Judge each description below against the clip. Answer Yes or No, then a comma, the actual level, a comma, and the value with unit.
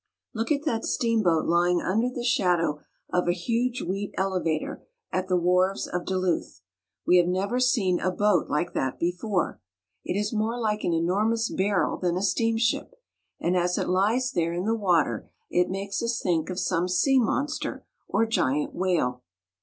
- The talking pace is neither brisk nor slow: Yes, average, 170 wpm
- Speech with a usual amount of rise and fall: Yes, average, 4.2 semitones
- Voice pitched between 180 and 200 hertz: Yes, medium, 185 Hz